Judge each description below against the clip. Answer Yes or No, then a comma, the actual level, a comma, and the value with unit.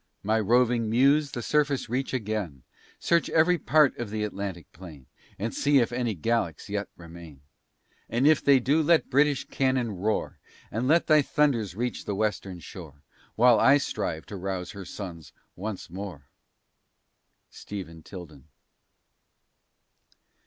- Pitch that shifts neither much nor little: No, wide, 6.3 semitones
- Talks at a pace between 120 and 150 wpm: Yes, average, 145 wpm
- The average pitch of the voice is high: No, low, 110 Hz